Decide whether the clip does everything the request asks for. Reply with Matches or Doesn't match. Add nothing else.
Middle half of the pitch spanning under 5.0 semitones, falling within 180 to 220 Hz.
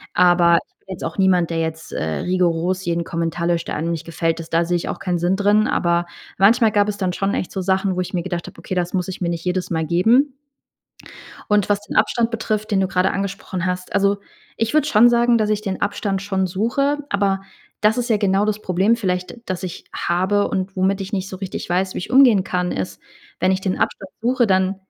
Matches